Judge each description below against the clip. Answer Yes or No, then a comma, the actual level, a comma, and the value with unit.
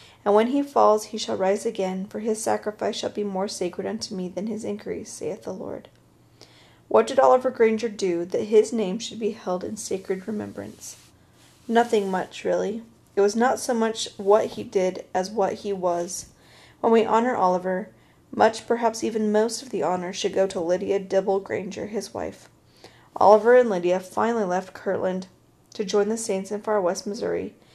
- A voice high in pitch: Yes, high, 205 Hz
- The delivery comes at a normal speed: Yes, average, 185 wpm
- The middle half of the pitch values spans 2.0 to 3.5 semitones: Yes, average, 2.9 semitones